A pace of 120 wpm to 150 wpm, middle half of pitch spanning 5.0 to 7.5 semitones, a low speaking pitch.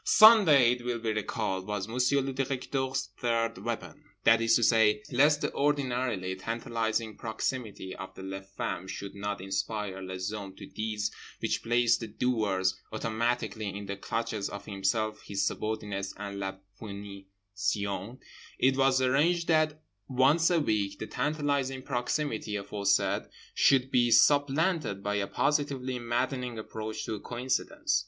No: average, 140 wpm; average, 4.4 semitones; low, 115 Hz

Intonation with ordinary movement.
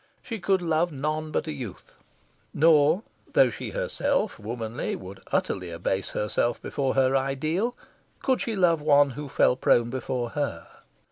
No: wide, 6.0 semitones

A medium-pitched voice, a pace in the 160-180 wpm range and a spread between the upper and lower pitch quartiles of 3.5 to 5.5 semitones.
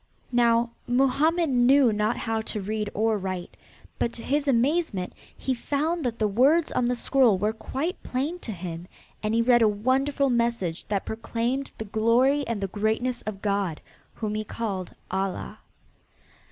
No: high, 230 Hz; average, 165 wpm; average, 3.9 semitones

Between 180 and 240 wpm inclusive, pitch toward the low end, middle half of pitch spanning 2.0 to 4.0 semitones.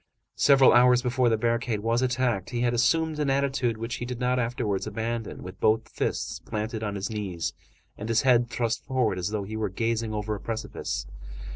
Yes: average, 195 wpm; low, 115 Hz; narrow, 2.5 semitones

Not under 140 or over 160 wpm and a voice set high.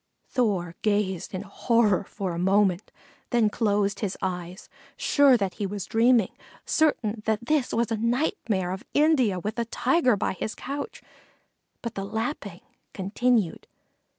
Yes: average, 145 wpm; high, 210 Hz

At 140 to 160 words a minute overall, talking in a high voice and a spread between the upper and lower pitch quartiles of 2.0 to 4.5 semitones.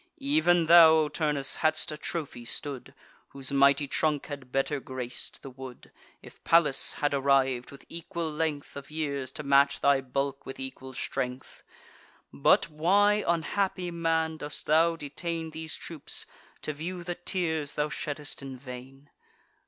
No: average, 150 wpm; medium, 150 Hz; average, 3.1 semitones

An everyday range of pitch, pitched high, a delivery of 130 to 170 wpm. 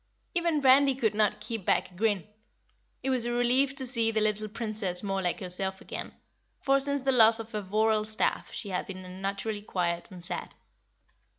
No: average, 4.3 semitones; high, 215 Hz; average, 190 wpm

